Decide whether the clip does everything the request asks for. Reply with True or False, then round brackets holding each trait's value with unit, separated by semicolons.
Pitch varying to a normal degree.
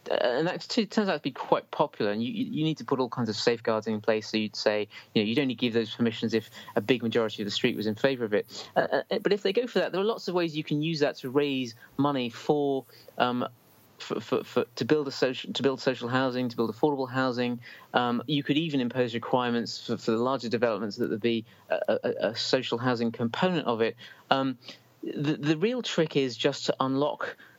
True (4.2 semitones)